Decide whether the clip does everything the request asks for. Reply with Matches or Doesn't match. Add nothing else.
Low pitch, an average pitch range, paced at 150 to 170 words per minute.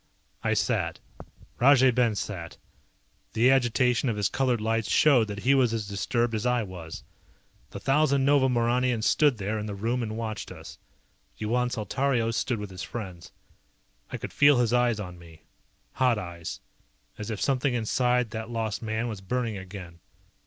Matches